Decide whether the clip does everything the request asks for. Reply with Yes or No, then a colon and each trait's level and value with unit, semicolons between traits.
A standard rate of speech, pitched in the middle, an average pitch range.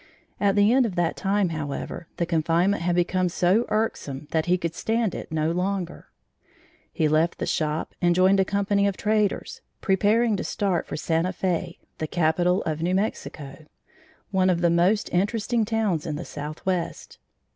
Yes: average, 170 wpm; medium, 180 Hz; average, 3.4 semitones